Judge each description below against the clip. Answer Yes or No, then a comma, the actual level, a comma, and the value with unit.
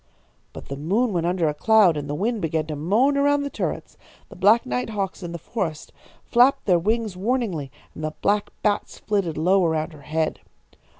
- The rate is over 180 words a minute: Yes, average, 195 wpm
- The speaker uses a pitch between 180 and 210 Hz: Yes, medium, 185 Hz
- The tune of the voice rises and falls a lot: Yes, wide, 5.8 semitones